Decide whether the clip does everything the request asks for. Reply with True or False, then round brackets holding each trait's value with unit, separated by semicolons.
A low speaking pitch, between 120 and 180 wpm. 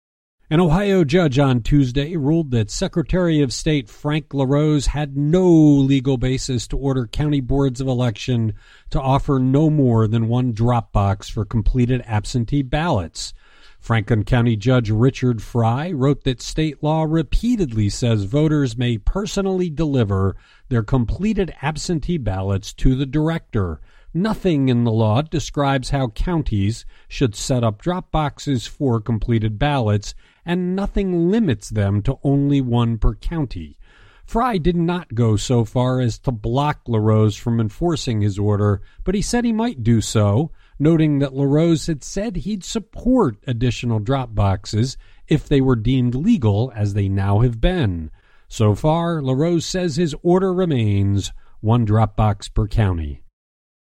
True (130 Hz; 150 wpm)